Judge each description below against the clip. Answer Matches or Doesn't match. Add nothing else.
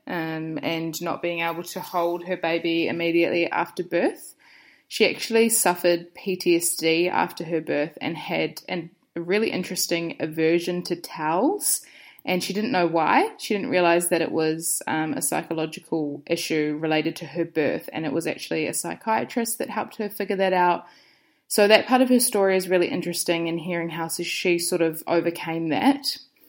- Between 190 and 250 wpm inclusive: Doesn't match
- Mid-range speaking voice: Matches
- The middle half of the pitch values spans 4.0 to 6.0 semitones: Doesn't match